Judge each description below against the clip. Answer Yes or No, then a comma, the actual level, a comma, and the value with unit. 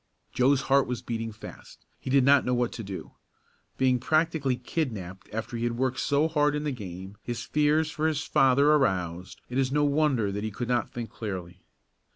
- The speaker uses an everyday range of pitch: Yes, average, 4.7 semitones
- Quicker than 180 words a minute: Yes, average, 195 wpm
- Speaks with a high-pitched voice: No, low, 125 Hz